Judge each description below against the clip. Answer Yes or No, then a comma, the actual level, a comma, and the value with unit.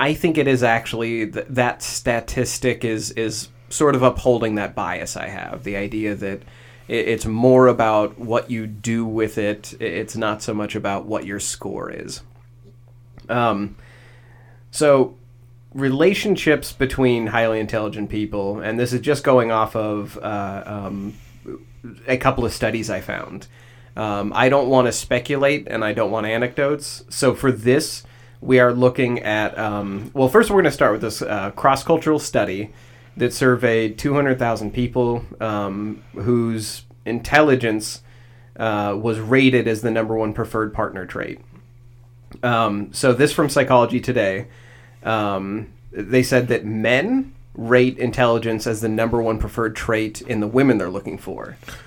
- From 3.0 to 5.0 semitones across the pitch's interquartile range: No, narrow, 2.4 semitones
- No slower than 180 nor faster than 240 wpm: No, average, 155 wpm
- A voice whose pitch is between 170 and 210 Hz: No, low, 120 Hz